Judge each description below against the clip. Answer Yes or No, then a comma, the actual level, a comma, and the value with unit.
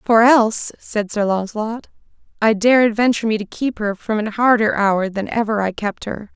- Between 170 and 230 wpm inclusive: Yes, average, 200 wpm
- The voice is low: No, high, 215 Hz